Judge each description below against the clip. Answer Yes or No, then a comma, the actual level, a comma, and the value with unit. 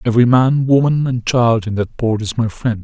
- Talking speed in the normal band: No, fast, 235 wpm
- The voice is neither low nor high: No, low, 120 Hz